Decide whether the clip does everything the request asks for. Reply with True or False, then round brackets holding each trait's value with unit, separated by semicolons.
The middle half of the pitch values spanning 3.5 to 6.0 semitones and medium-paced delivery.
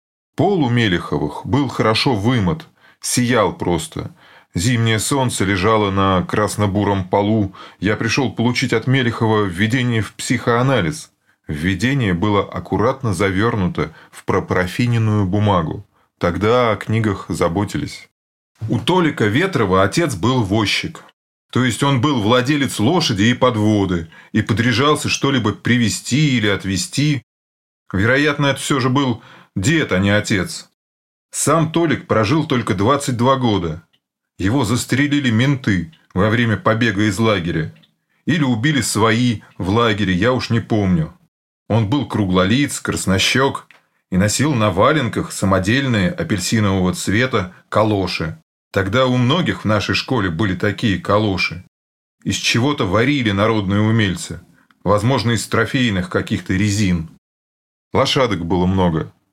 True (4.7 semitones; 120 wpm)